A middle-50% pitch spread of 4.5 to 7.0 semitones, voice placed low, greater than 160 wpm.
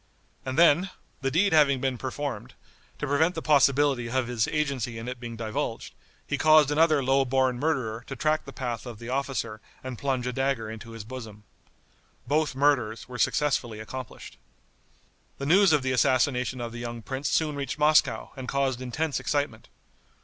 No: average, 3.4 semitones; low, 130 Hz; average, 175 wpm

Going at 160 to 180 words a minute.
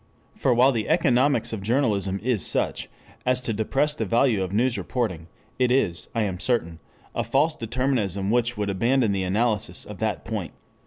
Yes: average, 175 wpm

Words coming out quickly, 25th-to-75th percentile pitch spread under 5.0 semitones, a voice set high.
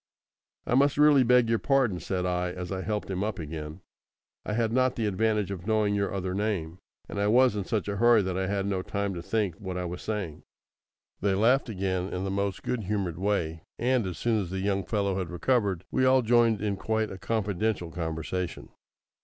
No: fast, 210 wpm; average, 3.3 semitones; low, 100 Hz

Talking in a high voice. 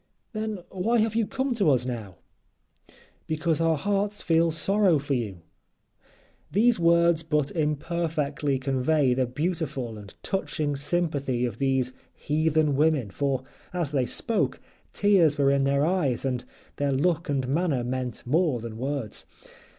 No: medium, 150 Hz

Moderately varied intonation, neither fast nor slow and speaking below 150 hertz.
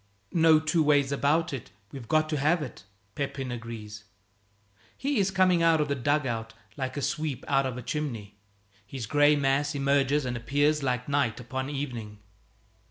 Yes: average, 3.3 semitones; average, 170 wpm; medium, 140 Hz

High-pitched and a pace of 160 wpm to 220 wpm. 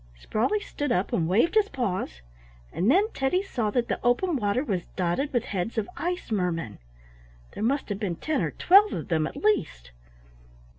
Yes: high, 230 Hz; average, 185 wpm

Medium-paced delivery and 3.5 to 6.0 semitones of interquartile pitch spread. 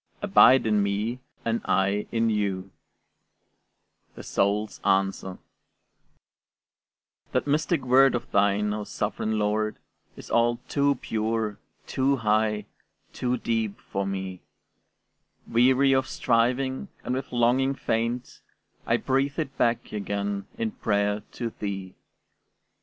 No: slow, 115 wpm; average, 3.9 semitones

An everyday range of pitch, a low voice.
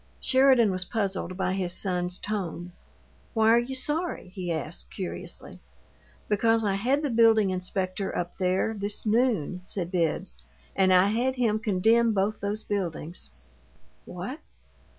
No: average, 3.9 semitones; high, 200 Hz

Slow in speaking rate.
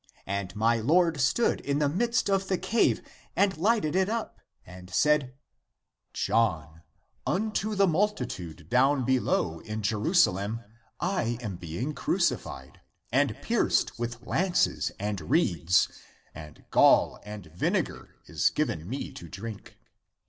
Yes: slow, 125 wpm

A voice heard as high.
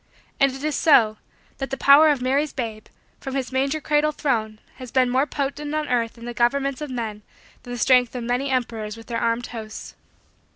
Yes: very high, 255 Hz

